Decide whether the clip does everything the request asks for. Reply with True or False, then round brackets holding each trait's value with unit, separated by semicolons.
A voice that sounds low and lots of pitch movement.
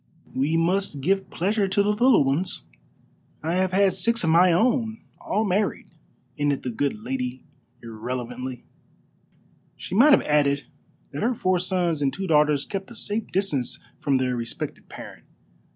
False (170 Hz; 6.3 semitones)